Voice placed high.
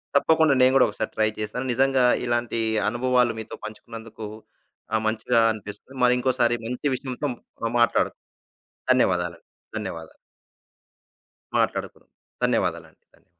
No: low, 120 Hz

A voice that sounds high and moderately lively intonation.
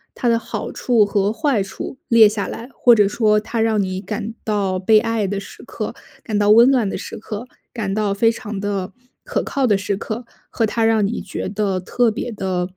No: high, 215 Hz; narrow, 2.3 semitones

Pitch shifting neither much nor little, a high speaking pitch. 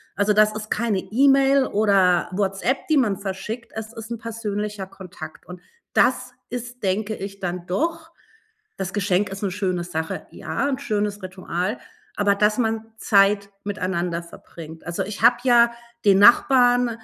Yes: average, 3.7 semitones; high, 210 Hz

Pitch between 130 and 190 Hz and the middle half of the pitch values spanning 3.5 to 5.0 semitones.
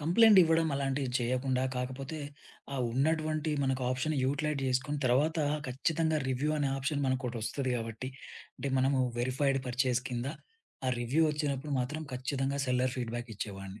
No: low, 135 Hz; average, 2.9 semitones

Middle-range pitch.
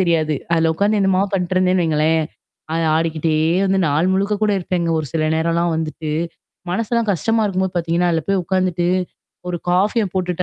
Yes: medium, 175 Hz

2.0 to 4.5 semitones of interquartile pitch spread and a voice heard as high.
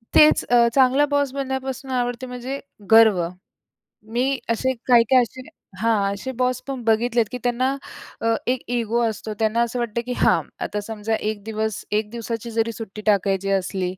Yes: average, 2.7 semitones; high, 235 Hz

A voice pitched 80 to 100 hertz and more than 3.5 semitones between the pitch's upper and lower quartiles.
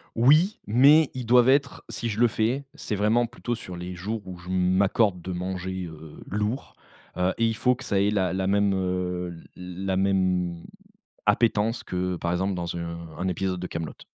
Yes: very low, 95 Hz; average, 4.0 semitones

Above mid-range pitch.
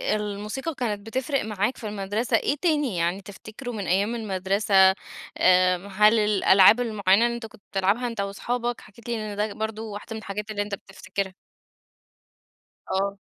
Yes: high, 210 Hz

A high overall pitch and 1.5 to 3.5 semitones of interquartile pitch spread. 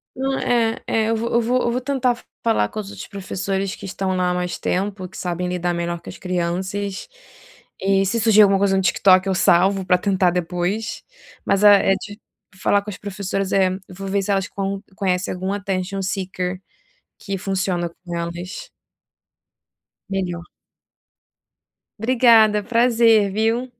Yes: high, 195 Hz; narrow, 2.5 semitones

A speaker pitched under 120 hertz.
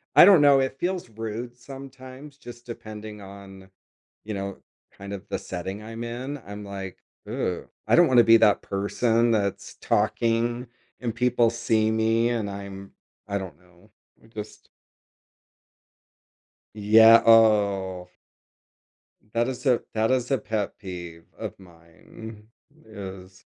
Yes: low, 110 Hz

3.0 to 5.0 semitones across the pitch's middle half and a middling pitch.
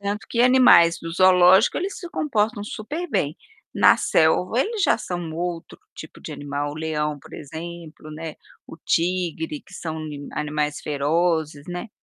Yes: average, 4.6 semitones; medium, 170 Hz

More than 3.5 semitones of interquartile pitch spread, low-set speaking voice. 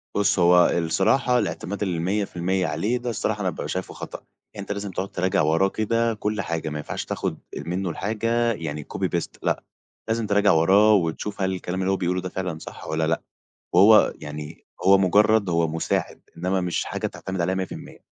No: average, 3.2 semitones; very low, 95 Hz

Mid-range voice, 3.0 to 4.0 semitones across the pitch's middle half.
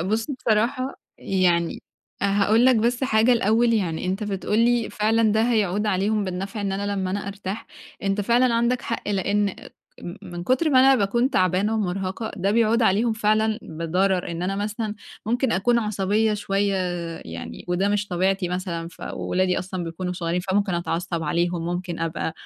No: high, 200 Hz; average, 3.3 semitones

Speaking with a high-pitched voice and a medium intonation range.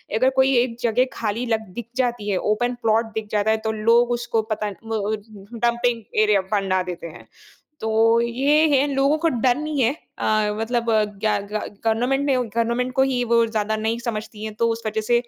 No: high, 230 Hz; narrow, 2.3 semitones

